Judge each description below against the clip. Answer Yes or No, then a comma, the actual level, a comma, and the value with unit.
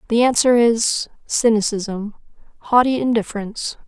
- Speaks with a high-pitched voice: Yes, high, 225 Hz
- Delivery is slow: Yes, slow, 75 wpm